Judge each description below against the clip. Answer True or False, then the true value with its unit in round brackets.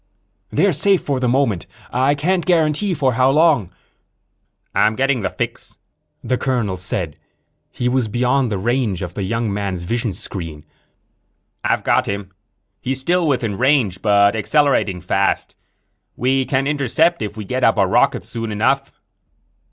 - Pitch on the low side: True (125 Hz)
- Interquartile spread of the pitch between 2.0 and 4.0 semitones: False (5.4 semitones)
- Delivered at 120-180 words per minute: True (150 wpm)